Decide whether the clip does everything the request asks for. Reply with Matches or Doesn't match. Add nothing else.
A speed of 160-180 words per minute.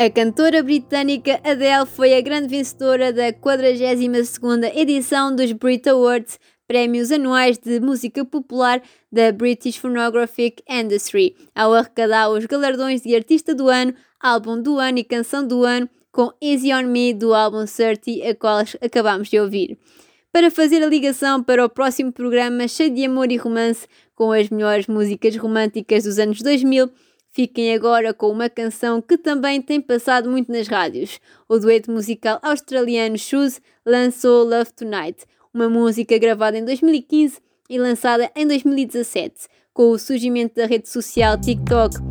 Doesn't match